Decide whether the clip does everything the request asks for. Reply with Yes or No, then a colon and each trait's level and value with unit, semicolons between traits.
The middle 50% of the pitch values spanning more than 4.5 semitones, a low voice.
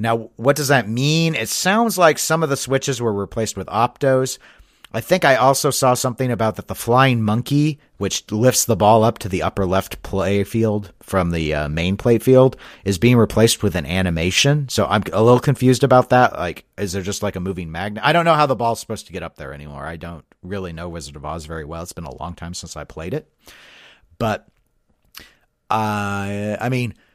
Yes: wide, 5.5 semitones; low, 110 Hz